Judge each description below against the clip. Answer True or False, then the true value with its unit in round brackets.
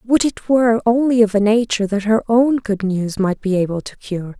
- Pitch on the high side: True (215 Hz)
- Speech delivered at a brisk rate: True (230 wpm)